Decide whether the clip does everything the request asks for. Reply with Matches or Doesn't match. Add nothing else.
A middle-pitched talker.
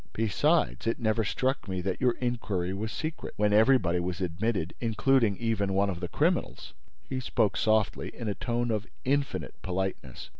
Doesn't match